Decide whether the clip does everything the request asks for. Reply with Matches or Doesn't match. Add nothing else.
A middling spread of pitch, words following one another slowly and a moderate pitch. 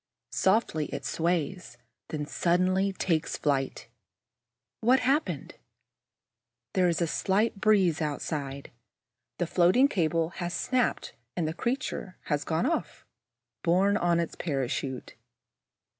Matches